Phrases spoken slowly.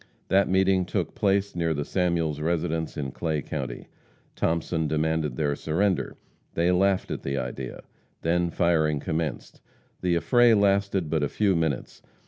No: average, 145 wpm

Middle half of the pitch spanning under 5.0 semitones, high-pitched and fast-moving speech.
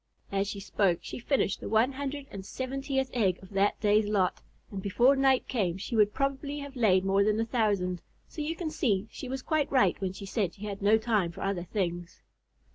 No: average, 5.3 semitones; high, 210 Hz; fast, 215 wpm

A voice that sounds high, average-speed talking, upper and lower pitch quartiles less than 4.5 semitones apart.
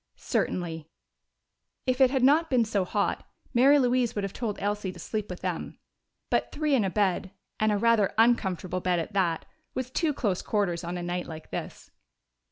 No: high, 205 Hz; average, 185 wpm; wide, 5.4 semitones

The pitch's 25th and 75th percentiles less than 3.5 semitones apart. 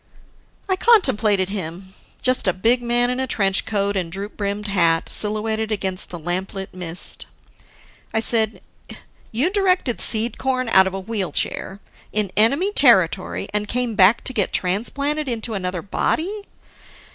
No: average, 4.4 semitones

